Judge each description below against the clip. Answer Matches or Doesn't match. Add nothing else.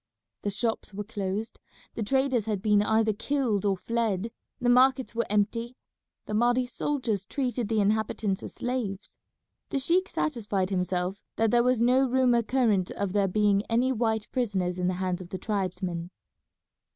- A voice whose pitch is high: Matches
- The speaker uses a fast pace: Doesn't match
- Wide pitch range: Doesn't match